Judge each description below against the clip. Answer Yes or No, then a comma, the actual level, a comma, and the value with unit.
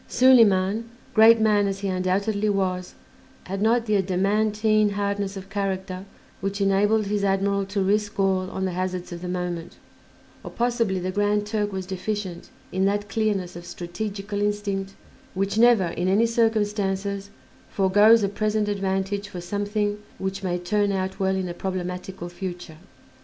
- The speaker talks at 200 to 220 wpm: No, average, 155 wpm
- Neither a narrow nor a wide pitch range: No, narrow, 1.8 semitones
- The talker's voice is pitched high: Yes, high, 195 Hz